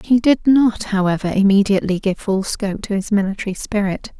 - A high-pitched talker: Yes, high, 205 Hz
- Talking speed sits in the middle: Yes, average, 170 wpm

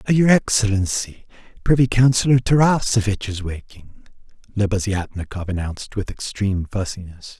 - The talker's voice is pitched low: Yes, low, 105 Hz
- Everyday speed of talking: No, slow, 95 wpm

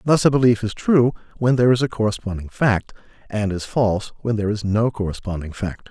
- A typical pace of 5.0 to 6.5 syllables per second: Yes, 5.9 syllables/s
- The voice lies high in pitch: No, low, 110 Hz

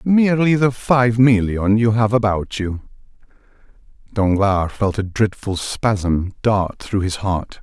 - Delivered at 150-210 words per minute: No, slow, 135 wpm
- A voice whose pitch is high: No, low, 110 Hz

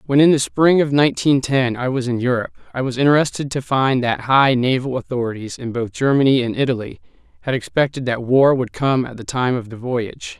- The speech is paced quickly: Yes, fast, 215 wpm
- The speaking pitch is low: Yes, low, 130 Hz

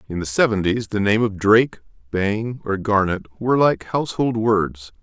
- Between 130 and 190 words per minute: Yes, average, 165 wpm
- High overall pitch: No, low, 105 Hz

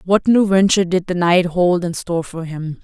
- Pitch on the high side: No, medium, 180 Hz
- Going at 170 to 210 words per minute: No, fast, 235 wpm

